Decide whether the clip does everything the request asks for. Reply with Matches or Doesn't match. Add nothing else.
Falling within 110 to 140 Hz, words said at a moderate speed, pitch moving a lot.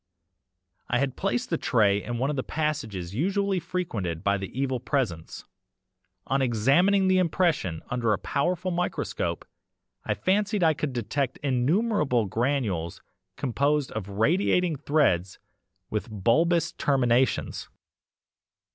Doesn't match